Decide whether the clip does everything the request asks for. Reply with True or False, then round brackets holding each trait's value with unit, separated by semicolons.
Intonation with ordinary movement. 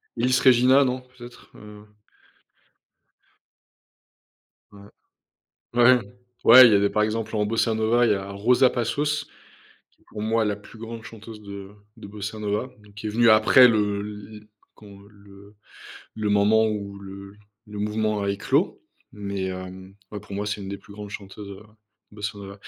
False (2.0 semitones)